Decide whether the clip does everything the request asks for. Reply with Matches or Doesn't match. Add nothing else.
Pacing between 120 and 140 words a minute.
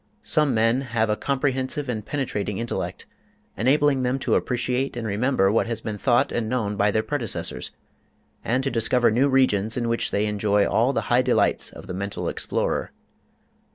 Doesn't match